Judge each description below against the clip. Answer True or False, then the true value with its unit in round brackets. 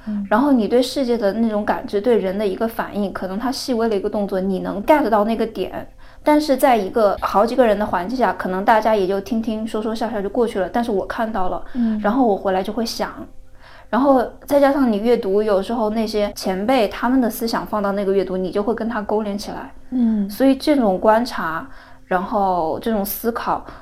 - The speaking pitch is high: True (215 Hz)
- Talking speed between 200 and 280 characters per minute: False (325 characters per minute)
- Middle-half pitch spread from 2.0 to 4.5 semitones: True (3.0 semitones)